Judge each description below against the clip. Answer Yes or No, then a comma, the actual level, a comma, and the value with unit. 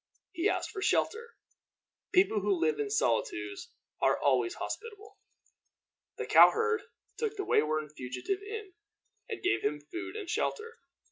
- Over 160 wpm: No, average, 140 wpm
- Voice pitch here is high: Yes, very high, 370 Hz